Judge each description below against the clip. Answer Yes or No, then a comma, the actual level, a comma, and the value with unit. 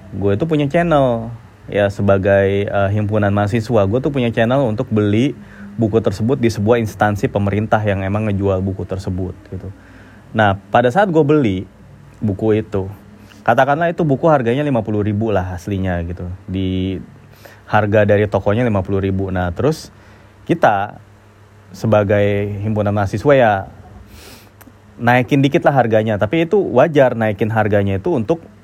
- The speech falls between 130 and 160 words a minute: Yes, average, 135 wpm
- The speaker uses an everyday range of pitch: Yes, average, 3.2 semitones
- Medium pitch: No, low, 105 Hz